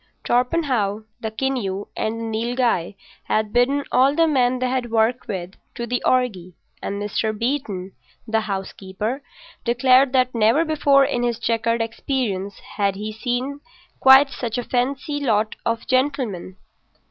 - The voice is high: Yes, high, 235 Hz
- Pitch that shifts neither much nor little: Yes, average, 3.4 semitones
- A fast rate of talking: No, average, 145 wpm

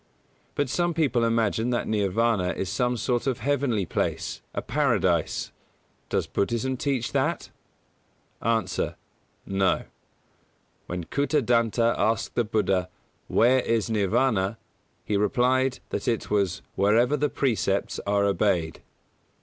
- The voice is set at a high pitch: No, low, 115 Hz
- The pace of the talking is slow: Yes, slow, 115 wpm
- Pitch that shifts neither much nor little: Yes, average, 4.0 semitones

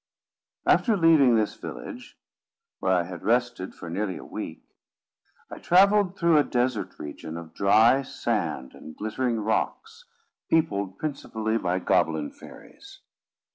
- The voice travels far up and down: Yes, wide, 7.9 semitones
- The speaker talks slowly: Yes, slow, 130 wpm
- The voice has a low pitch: Yes, low, 110 Hz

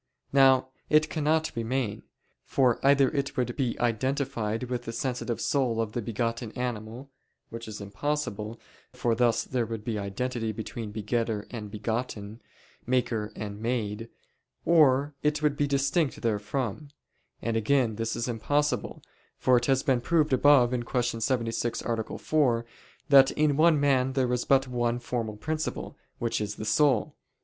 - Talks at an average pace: Yes, average, 150 wpm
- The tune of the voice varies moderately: Yes, average, 3.3 semitones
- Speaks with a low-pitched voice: Yes, low, 120 Hz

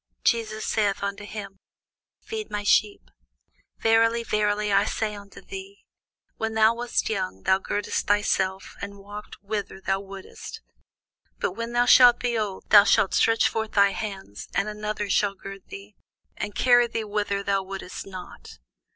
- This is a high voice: Yes, high, 210 Hz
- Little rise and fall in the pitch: Yes, narrow, 2.2 semitones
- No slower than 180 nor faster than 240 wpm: No, average, 155 wpm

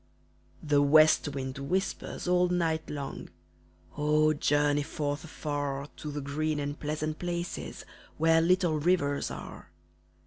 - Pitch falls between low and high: Yes, medium, 150 Hz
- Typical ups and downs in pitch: No, narrow, 2.2 semitones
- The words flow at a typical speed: No, slow, 125 wpm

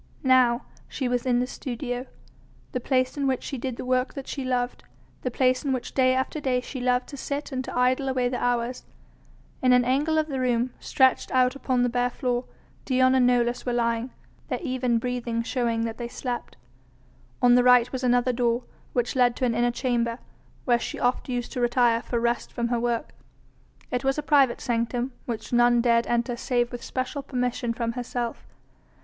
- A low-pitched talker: No, very high, 250 Hz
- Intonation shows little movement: Yes, narrow, 1.2 semitones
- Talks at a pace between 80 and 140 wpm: No, average, 200 wpm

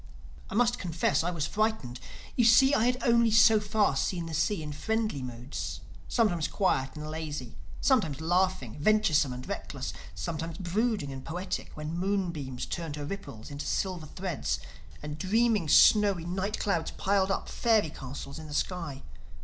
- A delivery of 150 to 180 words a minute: Yes, average, 160 wpm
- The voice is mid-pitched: Yes, medium, 175 Hz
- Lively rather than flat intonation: Yes, wide, 5.8 semitones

